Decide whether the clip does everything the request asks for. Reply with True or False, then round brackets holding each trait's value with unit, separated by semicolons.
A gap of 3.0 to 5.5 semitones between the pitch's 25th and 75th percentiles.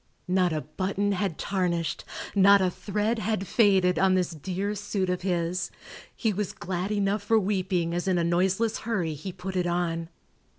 False (2.4 semitones)